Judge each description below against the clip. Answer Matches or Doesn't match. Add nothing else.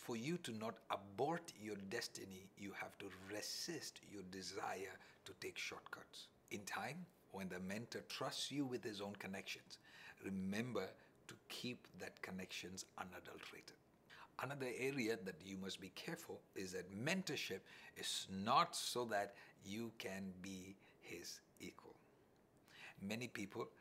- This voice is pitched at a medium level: Doesn't match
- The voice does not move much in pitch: Doesn't match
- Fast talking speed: Doesn't match